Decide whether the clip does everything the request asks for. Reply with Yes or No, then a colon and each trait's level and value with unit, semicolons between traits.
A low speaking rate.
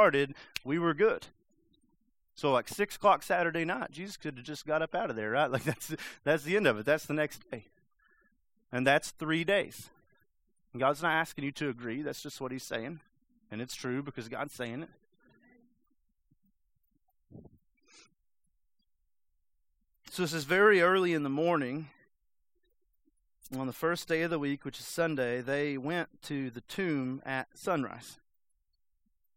No: average, 160 wpm